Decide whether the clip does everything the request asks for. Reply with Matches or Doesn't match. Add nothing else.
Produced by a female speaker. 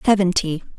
Matches